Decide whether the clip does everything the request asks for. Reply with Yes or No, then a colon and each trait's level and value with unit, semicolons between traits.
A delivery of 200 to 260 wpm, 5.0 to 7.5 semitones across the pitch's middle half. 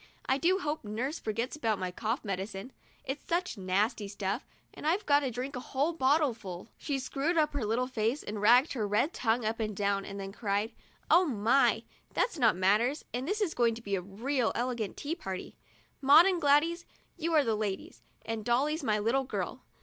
Yes: fast, 205 wpm; wide, 5.6 semitones